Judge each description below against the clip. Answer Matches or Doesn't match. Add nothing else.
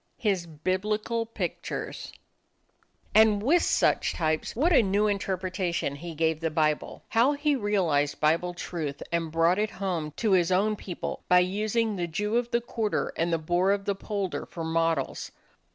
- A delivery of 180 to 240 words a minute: Doesn't match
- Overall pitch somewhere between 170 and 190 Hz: Matches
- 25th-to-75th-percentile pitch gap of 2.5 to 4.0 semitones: Doesn't match